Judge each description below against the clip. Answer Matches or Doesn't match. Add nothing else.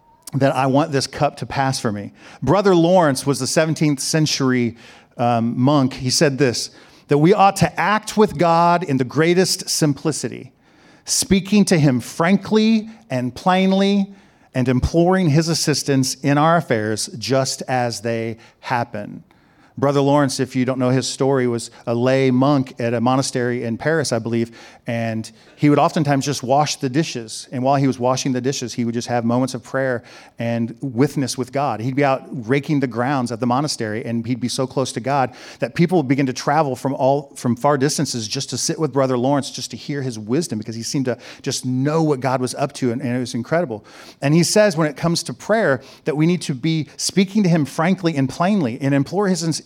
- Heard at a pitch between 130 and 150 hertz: Matches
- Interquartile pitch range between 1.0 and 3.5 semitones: Doesn't match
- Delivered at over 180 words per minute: Matches